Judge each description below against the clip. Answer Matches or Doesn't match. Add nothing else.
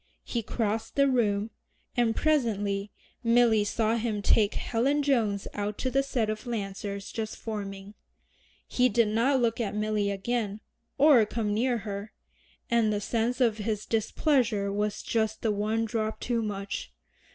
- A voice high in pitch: Matches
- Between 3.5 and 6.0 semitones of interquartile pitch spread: Doesn't match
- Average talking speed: Matches